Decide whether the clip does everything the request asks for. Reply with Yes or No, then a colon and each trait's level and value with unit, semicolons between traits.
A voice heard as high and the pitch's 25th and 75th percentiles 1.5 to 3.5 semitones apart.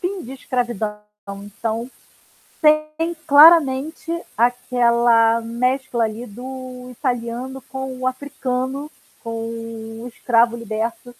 Yes: very high, 250 Hz; narrow, 2.4 semitones